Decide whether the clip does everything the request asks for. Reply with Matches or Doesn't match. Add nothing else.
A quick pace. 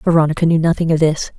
Matches